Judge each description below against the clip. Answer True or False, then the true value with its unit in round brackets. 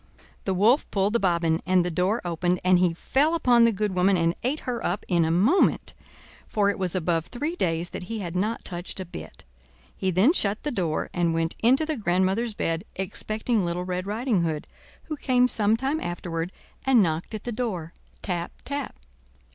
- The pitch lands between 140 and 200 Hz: True (190 Hz)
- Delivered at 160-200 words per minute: True (195 wpm)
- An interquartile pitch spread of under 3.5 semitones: False (5.1 semitones)